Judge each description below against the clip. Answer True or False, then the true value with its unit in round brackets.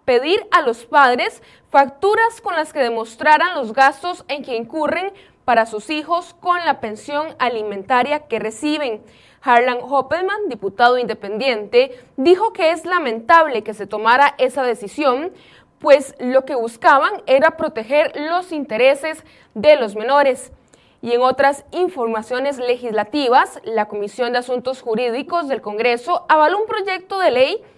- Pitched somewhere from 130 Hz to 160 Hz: False (275 Hz)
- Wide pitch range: True (5.7 semitones)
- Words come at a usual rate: True (140 wpm)